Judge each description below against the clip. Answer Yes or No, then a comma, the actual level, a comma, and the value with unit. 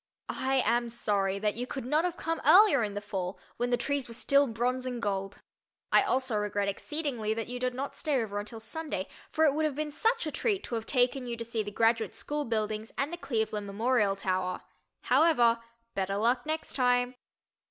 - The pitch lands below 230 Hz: No, high, 240 Hz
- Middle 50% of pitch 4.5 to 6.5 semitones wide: Yes, average, 4.8 semitones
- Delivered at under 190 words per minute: No, fast, 205 wpm